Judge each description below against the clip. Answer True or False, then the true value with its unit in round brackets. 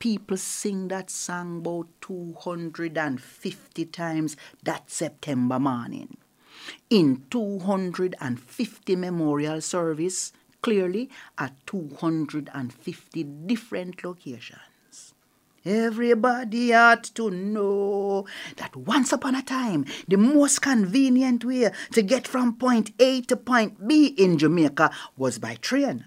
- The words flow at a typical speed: False (105 wpm)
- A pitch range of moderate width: False (6.4 semitones)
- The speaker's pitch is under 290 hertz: True (190 Hz)